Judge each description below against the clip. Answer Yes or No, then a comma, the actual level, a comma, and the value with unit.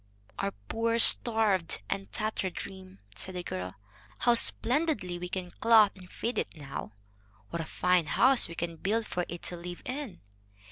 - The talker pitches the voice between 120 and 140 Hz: No, medium, 185 Hz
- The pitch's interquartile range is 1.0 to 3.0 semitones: No, average, 4.8 semitones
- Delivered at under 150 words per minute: No, average, 170 wpm